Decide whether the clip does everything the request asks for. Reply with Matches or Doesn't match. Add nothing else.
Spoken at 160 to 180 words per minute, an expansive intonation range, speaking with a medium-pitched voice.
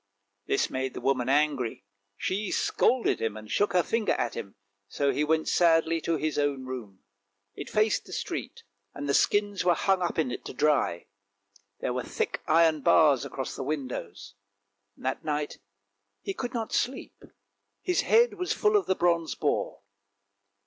Matches